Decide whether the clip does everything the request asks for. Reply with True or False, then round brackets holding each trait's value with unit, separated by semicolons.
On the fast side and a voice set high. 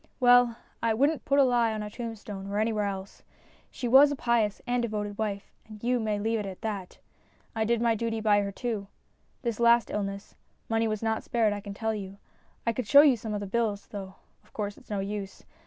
True (220 wpm; 220 Hz)